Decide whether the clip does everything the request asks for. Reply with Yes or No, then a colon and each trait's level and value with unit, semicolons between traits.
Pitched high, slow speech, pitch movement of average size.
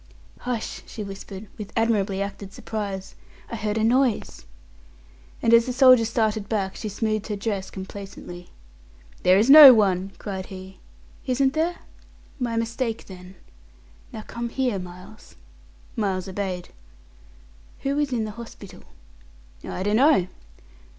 Yes: high, 215 Hz; slow, 130 wpm; average, 3.4 semitones